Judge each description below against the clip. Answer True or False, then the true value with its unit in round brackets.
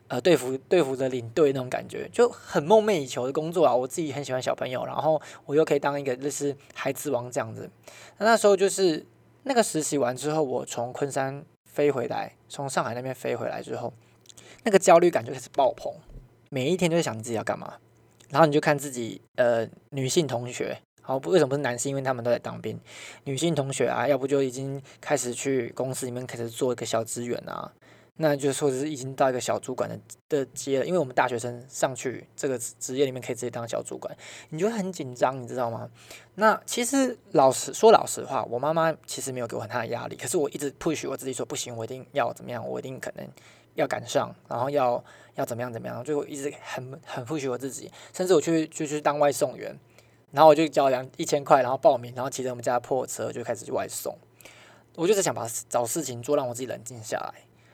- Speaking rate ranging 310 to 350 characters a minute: True (345 characters per minute)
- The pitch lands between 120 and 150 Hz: True (135 Hz)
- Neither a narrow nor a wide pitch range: True (3.9 semitones)